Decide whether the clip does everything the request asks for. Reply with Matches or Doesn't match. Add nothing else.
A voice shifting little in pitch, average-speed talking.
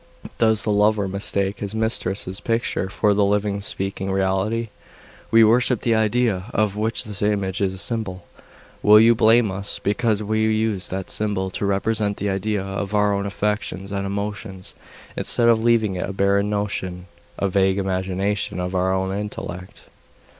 Matches